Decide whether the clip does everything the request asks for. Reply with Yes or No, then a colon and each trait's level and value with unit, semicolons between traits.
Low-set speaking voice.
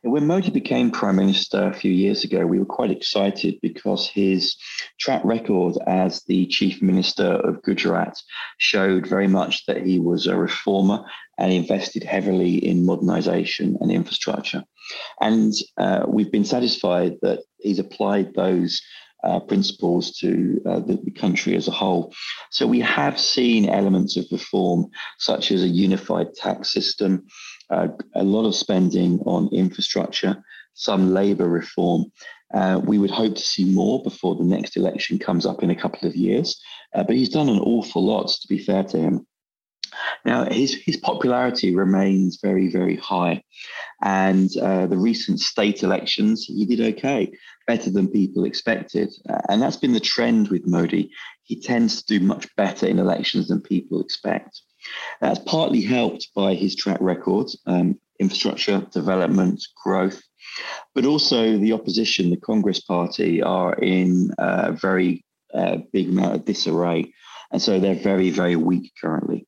Yes: very low, 95 Hz